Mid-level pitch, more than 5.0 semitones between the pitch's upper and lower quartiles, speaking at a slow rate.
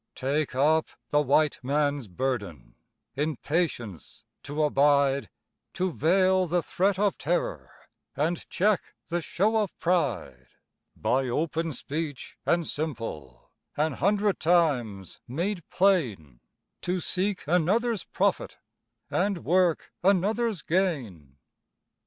Yes: medium, 160 Hz; wide, 5.5 semitones; slow, 110 wpm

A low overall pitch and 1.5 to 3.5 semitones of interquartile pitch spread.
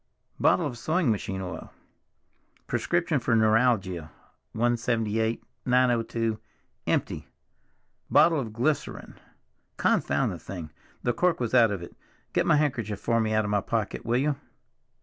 Yes: low, 115 Hz; average, 2.8 semitones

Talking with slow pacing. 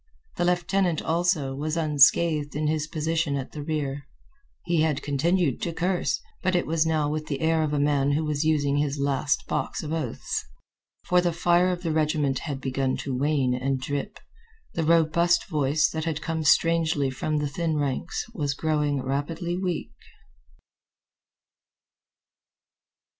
No: average, 160 wpm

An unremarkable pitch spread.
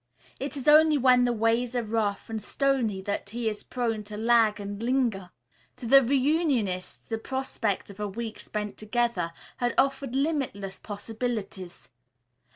Yes: average, 3.8 semitones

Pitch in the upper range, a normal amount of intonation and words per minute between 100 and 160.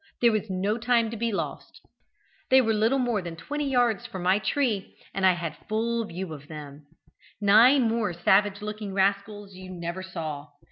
No: high, 205 Hz; average, 3.8 semitones; average, 185 wpm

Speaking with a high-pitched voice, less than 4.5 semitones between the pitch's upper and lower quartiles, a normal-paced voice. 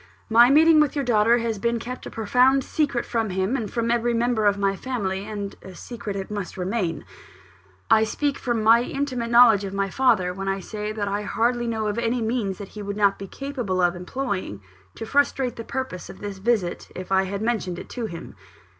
No: high, 220 Hz; average, 3.5 semitones; fast, 215 wpm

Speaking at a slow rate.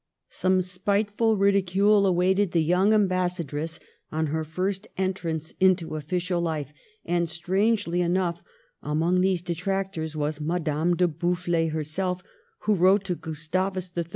Yes: slow, 130 wpm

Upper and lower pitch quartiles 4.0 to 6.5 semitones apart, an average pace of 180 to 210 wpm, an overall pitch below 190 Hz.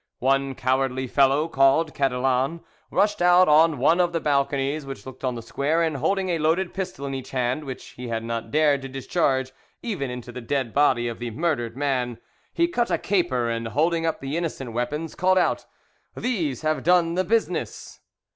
Yes: average, 4.5 semitones; average, 190 wpm; medium, 140 Hz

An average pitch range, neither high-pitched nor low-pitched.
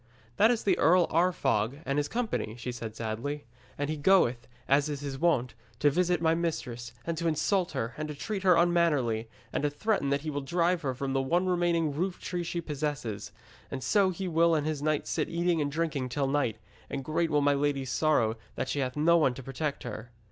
Yes: average, 4.1 semitones; medium, 150 Hz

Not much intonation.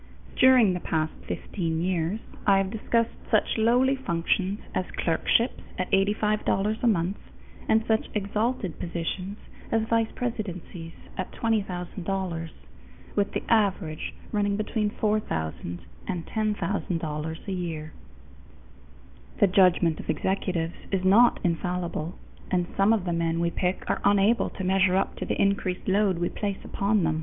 No: average, 3.7 semitones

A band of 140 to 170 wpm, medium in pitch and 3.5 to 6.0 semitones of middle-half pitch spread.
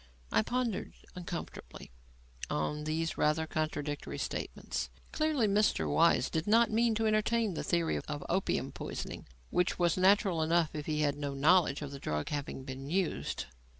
Yes: average, 155 wpm; medium, 165 Hz; wide, 5.5 semitones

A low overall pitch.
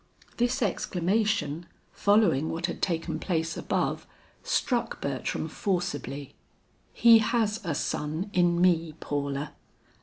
No: medium, 175 Hz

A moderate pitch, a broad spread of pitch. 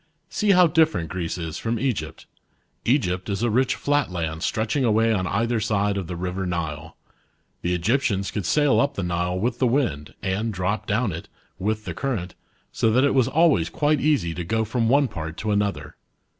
No: low, 105 Hz; wide, 6.2 semitones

